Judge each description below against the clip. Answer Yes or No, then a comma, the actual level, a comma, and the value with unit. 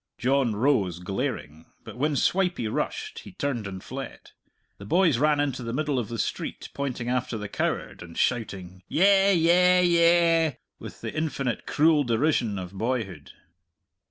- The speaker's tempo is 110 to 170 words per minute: Yes, average, 155 wpm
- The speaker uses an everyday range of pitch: No, wide, 6.8 semitones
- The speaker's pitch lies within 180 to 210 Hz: No, low, 130 Hz